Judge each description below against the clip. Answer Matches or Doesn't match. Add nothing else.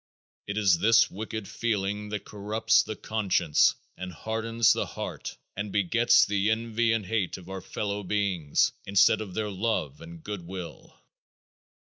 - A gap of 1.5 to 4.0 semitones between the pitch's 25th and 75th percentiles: Matches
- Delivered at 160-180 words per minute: Doesn't match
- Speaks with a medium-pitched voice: Doesn't match